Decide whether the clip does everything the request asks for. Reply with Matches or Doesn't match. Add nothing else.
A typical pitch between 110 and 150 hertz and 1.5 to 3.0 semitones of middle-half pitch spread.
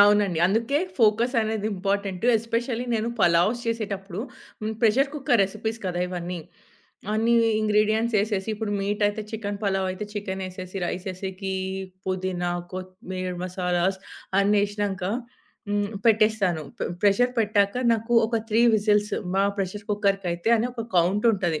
Doesn't match